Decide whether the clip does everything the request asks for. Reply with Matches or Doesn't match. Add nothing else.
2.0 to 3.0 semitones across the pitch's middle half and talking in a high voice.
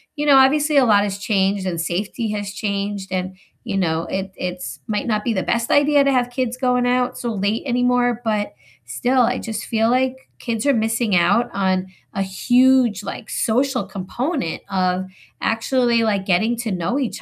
Doesn't match